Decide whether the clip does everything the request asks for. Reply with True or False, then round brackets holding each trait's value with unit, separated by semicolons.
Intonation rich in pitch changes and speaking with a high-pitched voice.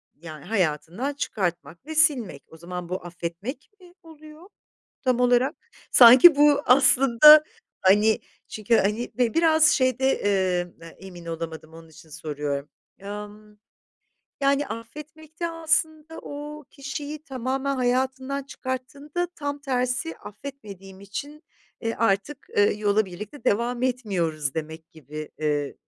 True (8.1 semitones; 235 Hz)